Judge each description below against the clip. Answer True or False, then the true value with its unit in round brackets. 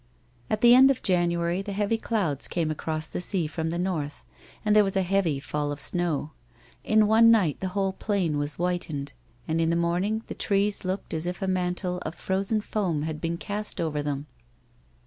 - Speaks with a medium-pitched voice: True (180 Hz)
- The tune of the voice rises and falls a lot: False (3.9 semitones)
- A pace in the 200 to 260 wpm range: True (205 wpm)